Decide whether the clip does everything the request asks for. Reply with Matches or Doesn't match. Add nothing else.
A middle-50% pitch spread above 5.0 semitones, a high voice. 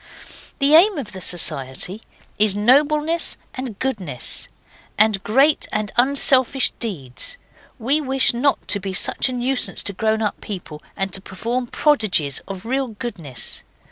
Matches